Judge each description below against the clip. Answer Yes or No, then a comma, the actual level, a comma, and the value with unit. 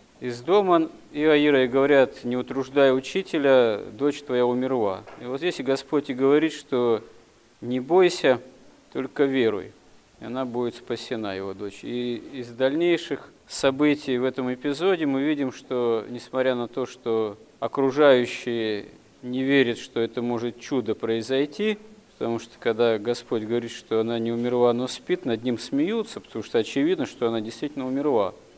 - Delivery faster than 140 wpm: Yes, average, 150 wpm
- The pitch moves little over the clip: No, average, 3.4 semitones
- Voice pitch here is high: No, low, 130 Hz